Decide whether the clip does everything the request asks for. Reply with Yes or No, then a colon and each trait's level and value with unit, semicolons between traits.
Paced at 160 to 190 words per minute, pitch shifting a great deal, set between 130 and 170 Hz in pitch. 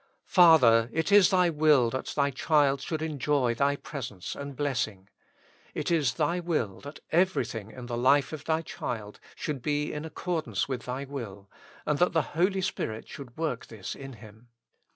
No: average, 175 wpm; average, 4.9 semitones; medium, 140 Hz